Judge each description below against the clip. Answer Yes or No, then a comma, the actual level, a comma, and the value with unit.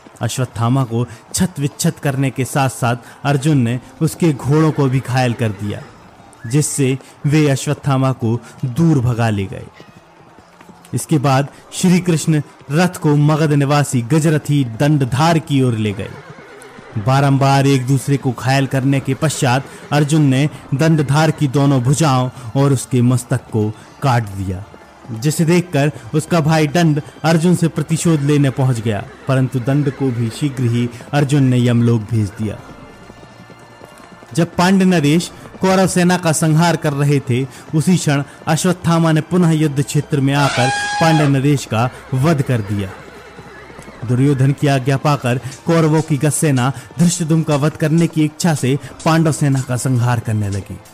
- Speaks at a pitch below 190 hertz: Yes, medium, 140 Hz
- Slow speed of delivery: No, average, 150 wpm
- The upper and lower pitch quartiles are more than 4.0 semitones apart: No, average, 3.7 semitones